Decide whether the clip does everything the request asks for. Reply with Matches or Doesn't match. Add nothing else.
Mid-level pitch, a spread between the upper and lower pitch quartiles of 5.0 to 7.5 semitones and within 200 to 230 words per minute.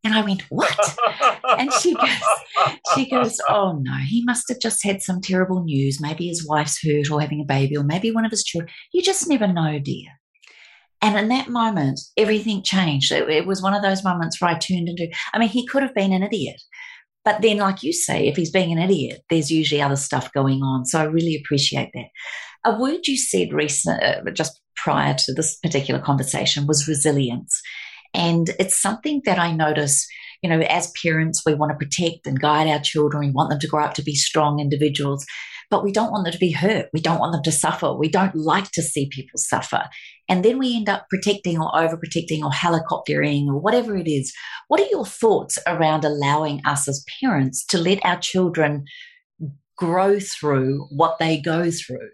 Matches